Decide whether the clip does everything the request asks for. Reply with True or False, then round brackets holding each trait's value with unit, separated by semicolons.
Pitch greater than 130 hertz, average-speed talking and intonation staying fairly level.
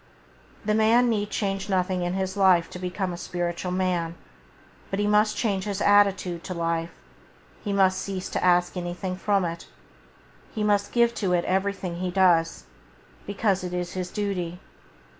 True (185 Hz; 175 wpm; 2.2 semitones)